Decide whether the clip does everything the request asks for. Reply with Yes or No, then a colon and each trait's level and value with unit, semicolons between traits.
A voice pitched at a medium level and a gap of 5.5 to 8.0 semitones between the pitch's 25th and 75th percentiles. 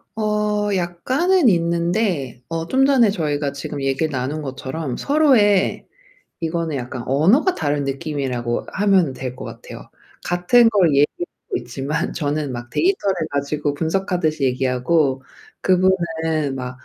Yes: medium, 160 Hz; wide, 6.0 semitones